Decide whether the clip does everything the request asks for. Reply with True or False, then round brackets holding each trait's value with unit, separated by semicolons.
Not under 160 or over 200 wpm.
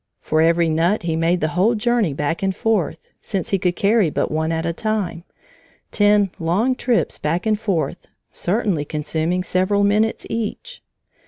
True (165 wpm)